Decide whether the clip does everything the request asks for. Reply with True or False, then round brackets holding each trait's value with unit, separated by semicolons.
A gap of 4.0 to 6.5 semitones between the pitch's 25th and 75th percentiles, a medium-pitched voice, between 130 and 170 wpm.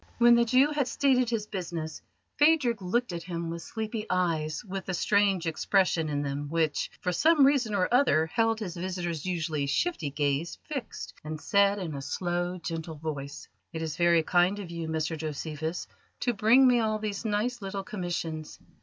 False (5.6 semitones; 180 Hz; 180 wpm)